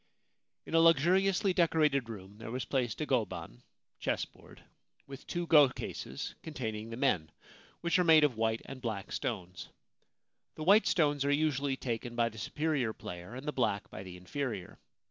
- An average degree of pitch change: No, wide, 5.7 semitones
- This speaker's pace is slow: No, average, 165 wpm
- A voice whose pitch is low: Yes, low, 130 Hz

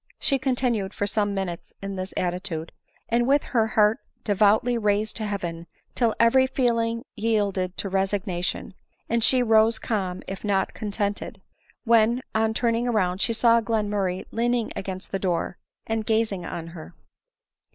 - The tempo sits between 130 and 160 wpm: Yes, average, 150 wpm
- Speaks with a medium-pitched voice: No, high, 215 Hz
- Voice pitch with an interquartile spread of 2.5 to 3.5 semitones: Yes, average, 3.1 semitones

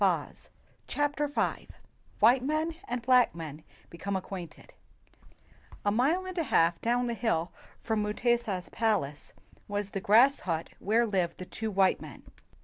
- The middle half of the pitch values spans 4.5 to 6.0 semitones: Yes, average, 5.0 semitones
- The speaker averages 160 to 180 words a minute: No, average, 145 wpm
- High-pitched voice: Yes, high, 220 Hz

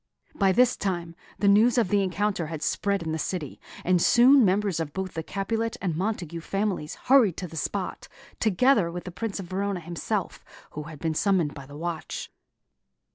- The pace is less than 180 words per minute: No, average, 185 wpm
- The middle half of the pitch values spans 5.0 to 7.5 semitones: No, average, 3.8 semitones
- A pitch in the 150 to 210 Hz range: Yes, medium, 185 Hz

